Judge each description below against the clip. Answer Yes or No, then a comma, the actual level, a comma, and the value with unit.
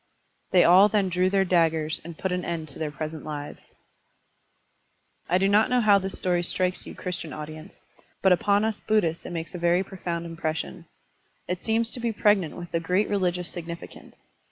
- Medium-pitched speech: Yes, medium, 180 Hz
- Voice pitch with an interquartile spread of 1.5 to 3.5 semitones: Yes, average, 3.0 semitones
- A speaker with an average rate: Yes, average, 185 wpm